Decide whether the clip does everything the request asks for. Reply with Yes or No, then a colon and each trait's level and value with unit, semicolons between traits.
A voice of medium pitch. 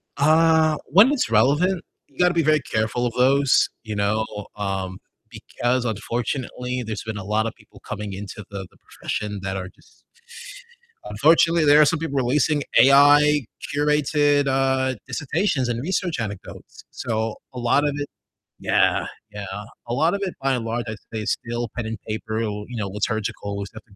No: low, 125 Hz